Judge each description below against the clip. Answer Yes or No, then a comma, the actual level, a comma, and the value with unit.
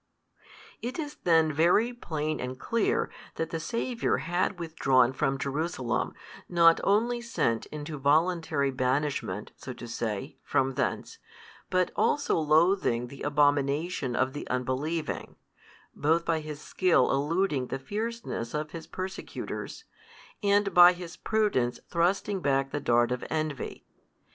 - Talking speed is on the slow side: Yes, slow, 130 wpm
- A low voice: No, medium, 155 Hz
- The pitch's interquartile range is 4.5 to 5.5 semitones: Yes, average, 5.1 semitones